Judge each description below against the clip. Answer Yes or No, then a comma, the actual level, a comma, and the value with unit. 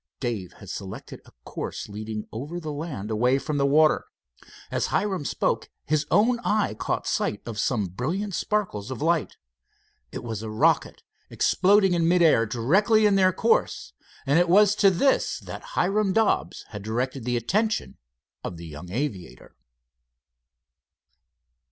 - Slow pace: No, average, 150 wpm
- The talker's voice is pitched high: No, medium, 150 Hz